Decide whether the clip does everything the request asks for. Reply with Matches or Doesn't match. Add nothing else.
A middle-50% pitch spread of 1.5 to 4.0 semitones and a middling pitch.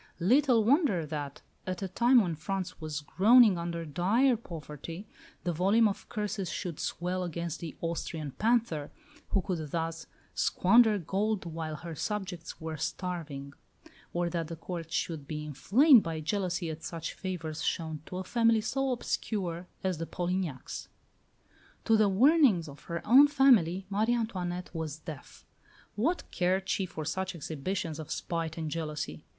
Doesn't match